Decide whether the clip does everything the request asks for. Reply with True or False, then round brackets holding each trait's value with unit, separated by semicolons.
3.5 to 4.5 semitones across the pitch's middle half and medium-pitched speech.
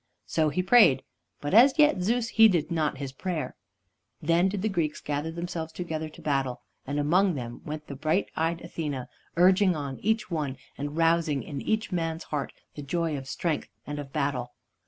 True (3.9 semitones; 160 Hz)